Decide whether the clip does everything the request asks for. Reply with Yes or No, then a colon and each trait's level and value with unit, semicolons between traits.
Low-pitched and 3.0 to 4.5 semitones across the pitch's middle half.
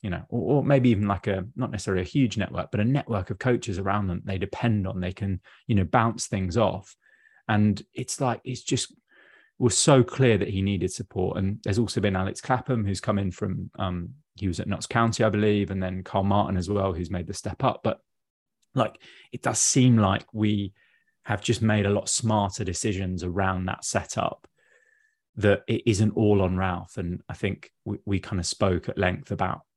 Yes: low, 100 Hz; average, 3.3 semitones